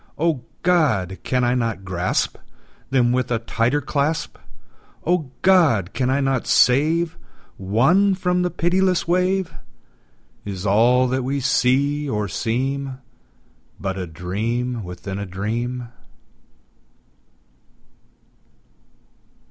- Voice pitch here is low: Yes, low, 125 Hz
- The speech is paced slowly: Yes, slow, 110 wpm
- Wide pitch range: Yes, wide, 6.3 semitones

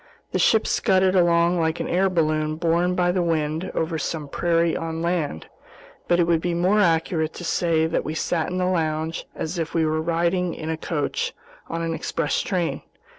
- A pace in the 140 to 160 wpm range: No, average, 195 wpm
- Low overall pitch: No, medium, 165 Hz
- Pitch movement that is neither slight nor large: No, narrow, 1.8 semitones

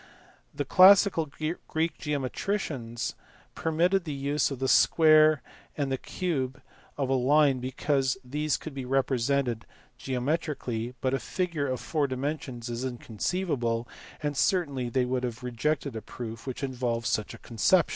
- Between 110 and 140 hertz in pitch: Yes, low, 135 Hz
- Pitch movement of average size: Yes, average, 3.7 semitones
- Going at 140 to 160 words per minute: Yes, average, 145 wpm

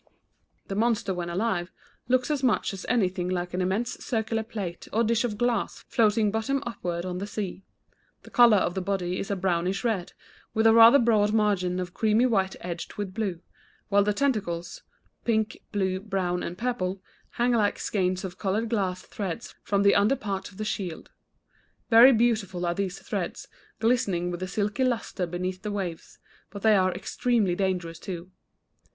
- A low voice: No, high, 200 Hz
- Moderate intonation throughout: Yes, average, 3.6 semitones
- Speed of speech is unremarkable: Yes, average, 175 wpm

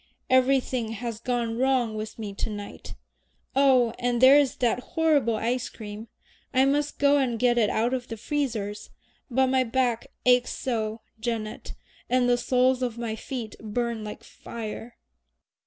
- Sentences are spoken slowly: No, average, 155 wpm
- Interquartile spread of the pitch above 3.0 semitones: No, narrow, 2.6 semitones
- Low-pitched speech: No, high, 240 Hz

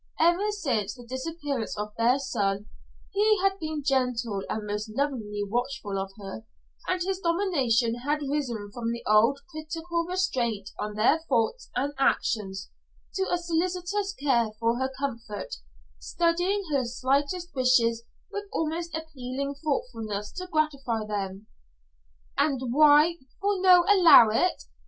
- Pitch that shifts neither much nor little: No, wide, 6.8 semitones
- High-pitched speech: Yes, very high, 270 Hz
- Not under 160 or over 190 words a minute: No, slow, 135 wpm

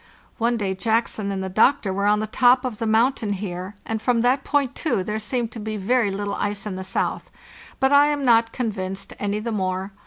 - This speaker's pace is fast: Yes, fast, 220 wpm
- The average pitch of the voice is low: No, high, 215 Hz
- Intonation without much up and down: No, average, 3.5 semitones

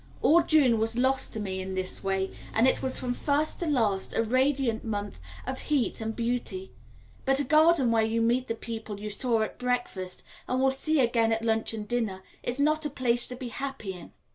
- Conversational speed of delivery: No, fast, 215 wpm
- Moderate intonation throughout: Yes, average, 3.4 semitones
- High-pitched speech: Yes, high, 240 Hz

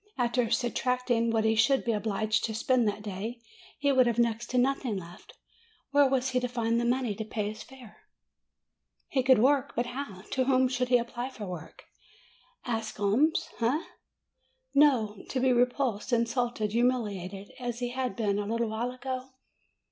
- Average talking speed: Yes, average, 180 wpm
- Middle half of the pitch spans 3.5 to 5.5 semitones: No, average, 2.8 semitones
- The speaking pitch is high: Yes, high, 240 Hz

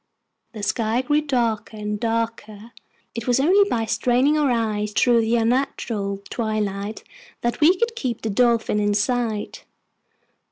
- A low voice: No, high, 230 Hz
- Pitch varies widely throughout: No, average, 2.8 semitones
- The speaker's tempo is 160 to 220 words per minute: No, average, 145 wpm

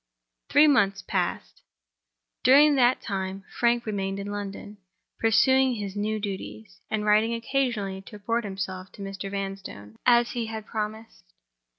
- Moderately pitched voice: No, high, 210 Hz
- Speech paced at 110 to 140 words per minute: Yes, slow, 135 wpm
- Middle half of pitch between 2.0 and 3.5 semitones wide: Yes, average, 3.1 semitones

